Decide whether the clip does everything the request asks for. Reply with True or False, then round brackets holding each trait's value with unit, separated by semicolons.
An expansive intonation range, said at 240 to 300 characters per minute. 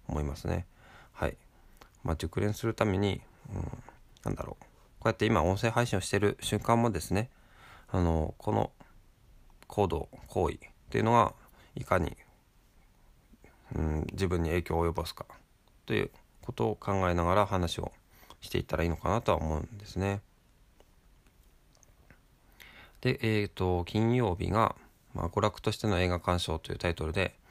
False (3.9 semitones; 290 characters per minute)